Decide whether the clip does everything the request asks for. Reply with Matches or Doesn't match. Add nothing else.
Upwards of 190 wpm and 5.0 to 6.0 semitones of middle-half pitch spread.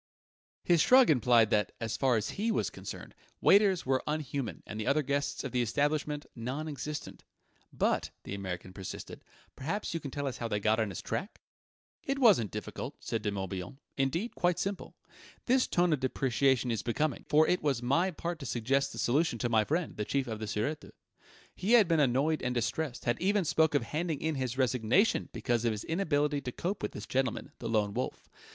Matches